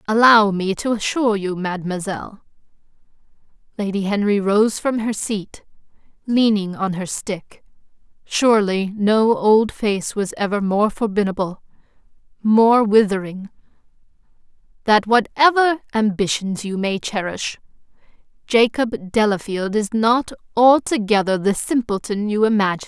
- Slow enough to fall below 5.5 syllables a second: Yes, 4.5 syllables/s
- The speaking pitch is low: No, high, 210 Hz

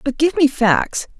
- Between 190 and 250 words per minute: Yes, average, 200 wpm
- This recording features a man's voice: No, female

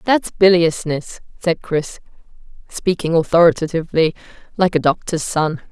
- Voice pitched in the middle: Yes, medium, 165 Hz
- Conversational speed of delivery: No, slow, 105 wpm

